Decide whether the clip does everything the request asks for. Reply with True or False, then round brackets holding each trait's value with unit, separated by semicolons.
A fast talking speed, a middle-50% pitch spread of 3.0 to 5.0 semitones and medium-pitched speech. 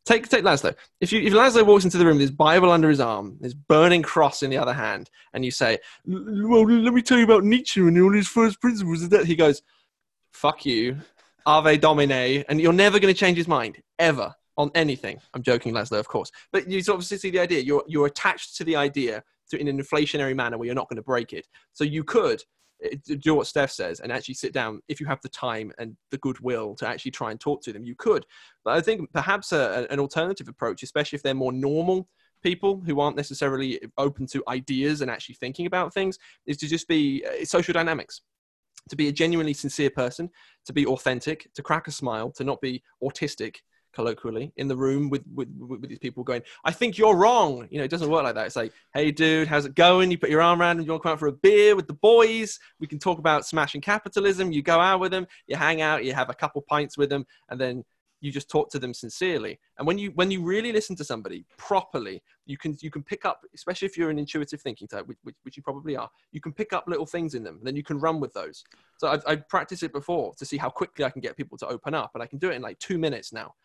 True (250 wpm; 4.7 semitones; 150 Hz)